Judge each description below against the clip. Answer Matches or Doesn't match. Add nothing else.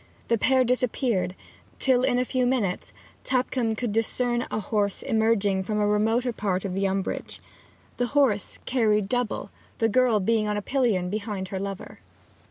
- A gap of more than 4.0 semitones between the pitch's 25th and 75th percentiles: Doesn't match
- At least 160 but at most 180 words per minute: Matches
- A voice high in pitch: Matches